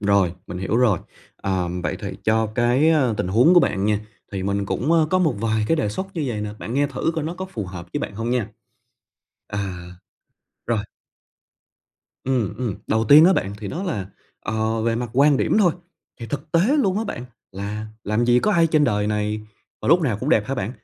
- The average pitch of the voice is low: Yes, low, 115 Hz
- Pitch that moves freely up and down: Yes, wide, 6.4 semitones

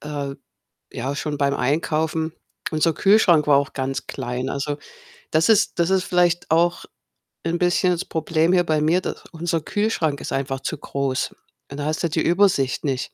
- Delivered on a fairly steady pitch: No, average, 3.6 semitones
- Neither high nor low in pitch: Yes, medium, 155 Hz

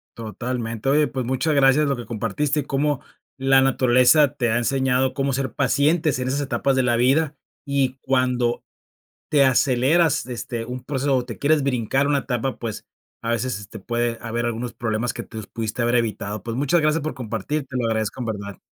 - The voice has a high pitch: No, low, 125 Hz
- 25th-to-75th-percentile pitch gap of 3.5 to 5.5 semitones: No, average, 2.9 semitones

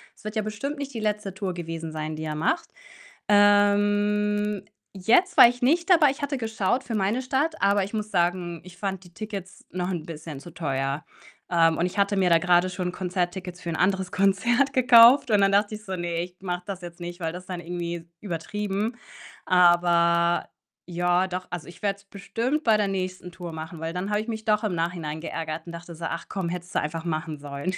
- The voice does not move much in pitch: No, average, 3.5 semitones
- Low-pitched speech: No, medium, 185 Hz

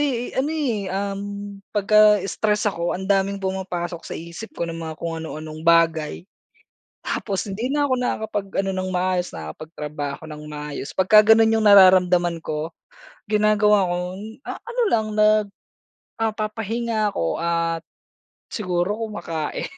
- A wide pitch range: No, average, 4.1 semitones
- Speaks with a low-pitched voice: No, high, 190 Hz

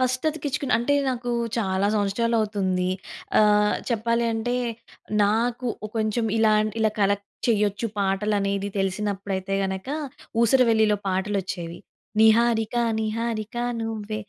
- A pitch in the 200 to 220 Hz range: Yes, high, 215 Hz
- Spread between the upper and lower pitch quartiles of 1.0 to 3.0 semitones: Yes, narrow, 2.6 semitones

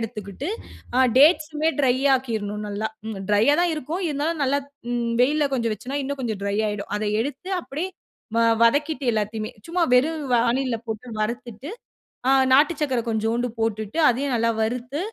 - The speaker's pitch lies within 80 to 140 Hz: No, very high, 250 Hz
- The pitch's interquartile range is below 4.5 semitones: No, average, 4.8 semitones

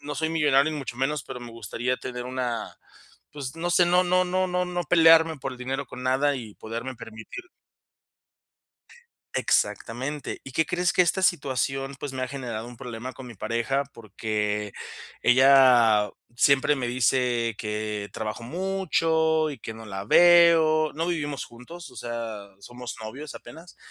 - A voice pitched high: No, low, 130 Hz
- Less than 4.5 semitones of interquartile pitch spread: No, average, 5.2 semitones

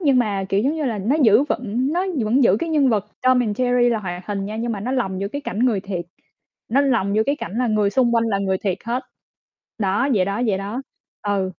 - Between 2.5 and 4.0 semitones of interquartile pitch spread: No, average, 4.4 semitones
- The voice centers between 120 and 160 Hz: No, high, 220 Hz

